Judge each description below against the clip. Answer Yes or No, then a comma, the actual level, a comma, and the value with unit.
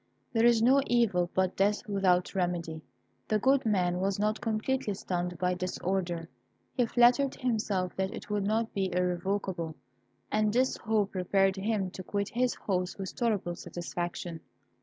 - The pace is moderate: Yes, average, 160 wpm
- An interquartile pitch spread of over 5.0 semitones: No, average, 3.5 semitones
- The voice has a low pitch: No, high, 195 Hz